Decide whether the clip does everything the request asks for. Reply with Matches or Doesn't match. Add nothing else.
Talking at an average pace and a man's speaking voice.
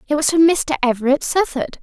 Doesn't match